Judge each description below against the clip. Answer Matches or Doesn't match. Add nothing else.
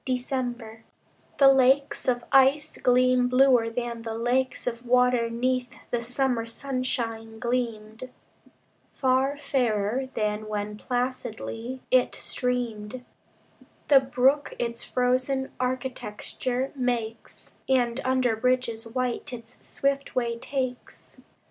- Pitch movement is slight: Matches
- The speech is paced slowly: Matches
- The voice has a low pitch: Doesn't match